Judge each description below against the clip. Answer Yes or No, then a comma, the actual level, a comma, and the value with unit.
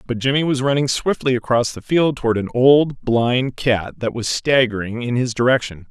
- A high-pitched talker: No, low, 125 Hz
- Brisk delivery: No, average, 195 wpm